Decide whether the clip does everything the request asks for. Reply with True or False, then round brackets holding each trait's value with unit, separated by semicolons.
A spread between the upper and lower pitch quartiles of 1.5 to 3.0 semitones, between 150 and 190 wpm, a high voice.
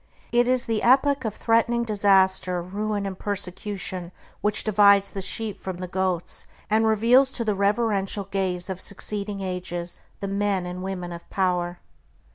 True (2.7 semitones; 155 wpm; 200 Hz)